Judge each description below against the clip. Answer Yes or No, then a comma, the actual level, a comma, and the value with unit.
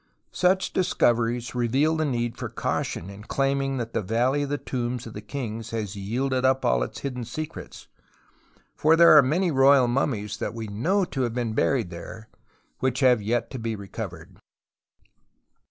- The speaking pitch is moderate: No, low, 125 Hz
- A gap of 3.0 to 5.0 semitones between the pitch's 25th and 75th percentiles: Yes, average, 3.5 semitones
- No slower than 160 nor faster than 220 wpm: Yes, average, 170 wpm